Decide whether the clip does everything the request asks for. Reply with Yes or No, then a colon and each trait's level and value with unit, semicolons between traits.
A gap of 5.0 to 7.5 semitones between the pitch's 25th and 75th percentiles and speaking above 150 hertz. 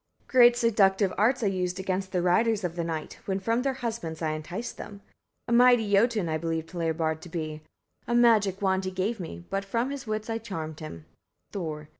Yes: wide, 5.5 semitones; high, 190 Hz